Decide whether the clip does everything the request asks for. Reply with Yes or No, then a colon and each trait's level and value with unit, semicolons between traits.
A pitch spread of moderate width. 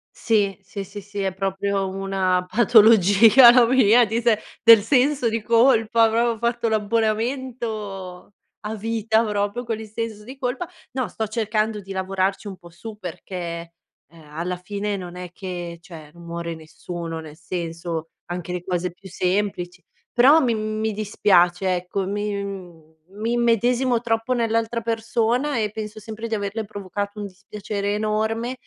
Yes: average, 3.5 semitones